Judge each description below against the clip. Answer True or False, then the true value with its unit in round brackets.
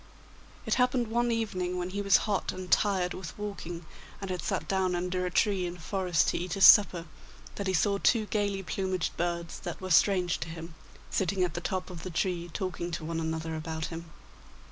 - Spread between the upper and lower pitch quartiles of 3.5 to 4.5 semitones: False (2.5 semitones)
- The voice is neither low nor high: True (180 Hz)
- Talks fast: True (210 wpm)